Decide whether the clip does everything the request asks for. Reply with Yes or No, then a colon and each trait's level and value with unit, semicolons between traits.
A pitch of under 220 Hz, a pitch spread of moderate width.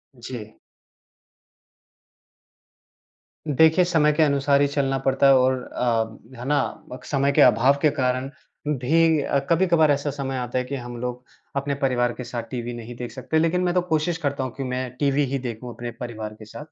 Yes: low, 135 Hz; average, 3.1 semitones